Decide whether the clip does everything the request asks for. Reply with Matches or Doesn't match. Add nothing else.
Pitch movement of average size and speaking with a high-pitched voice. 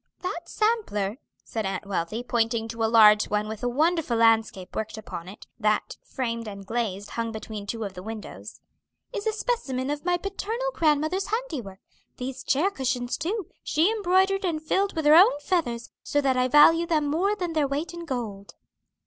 Doesn't match